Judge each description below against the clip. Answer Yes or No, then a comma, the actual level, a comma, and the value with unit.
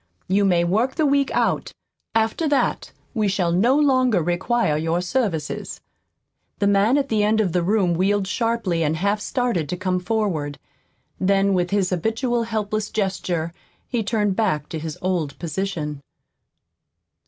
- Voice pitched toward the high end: Yes, high, 195 Hz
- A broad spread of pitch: No, average, 4.3 semitones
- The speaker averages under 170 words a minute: Yes, average, 155 wpm